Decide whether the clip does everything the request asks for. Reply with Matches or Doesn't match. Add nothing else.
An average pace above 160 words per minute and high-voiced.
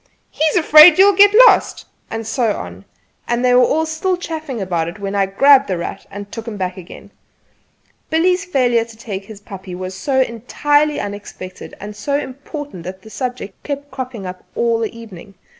Matches